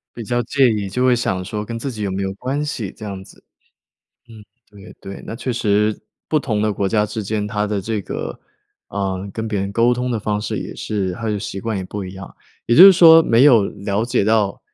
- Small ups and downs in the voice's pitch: No, average, 3.0 semitones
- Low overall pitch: Yes, low, 105 Hz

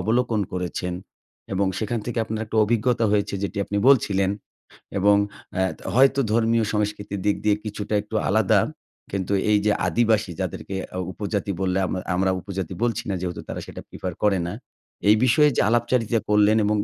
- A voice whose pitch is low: Yes, low, 105 Hz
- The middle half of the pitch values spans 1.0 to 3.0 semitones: Yes, narrow, 2.6 semitones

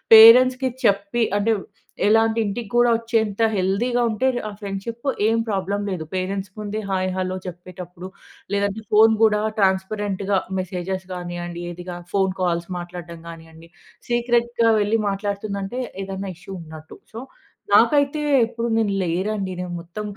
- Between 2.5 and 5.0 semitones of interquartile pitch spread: Yes, average, 3.5 semitones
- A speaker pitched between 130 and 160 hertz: No, high, 200 Hz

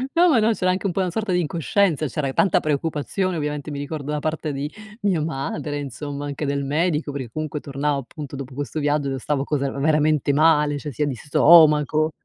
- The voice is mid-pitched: Yes, medium, 150 Hz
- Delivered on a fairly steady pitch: Yes, narrow, 2.2 semitones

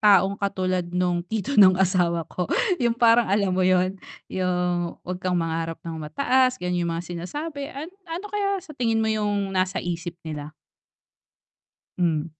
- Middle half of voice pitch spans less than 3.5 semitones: No, average, 4.2 semitones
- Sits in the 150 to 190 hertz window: Yes, medium, 185 Hz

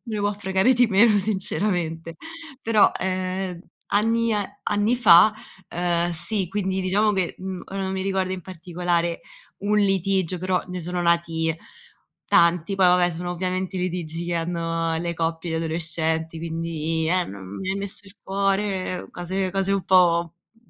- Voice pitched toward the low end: No, medium, 185 Hz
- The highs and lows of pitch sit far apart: No, narrow, 2.5 semitones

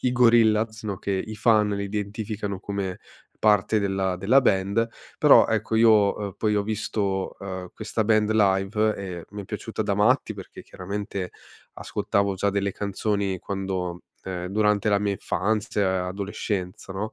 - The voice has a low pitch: Yes, low, 100 Hz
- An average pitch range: No, narrow, 2.0 semitones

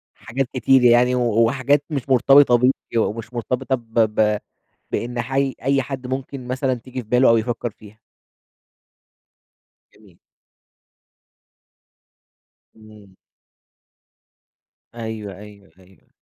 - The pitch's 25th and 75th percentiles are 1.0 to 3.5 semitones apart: Yes, average, 3.0 semitones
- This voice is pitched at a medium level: No, low, 120 Hz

